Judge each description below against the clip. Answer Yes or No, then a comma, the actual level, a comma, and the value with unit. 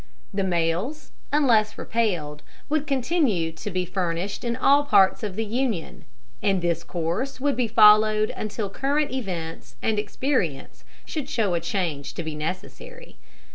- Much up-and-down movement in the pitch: Yes, wide, 6.9 semitones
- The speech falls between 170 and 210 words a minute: No, average, 145 wpm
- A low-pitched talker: No, high, 210 Hz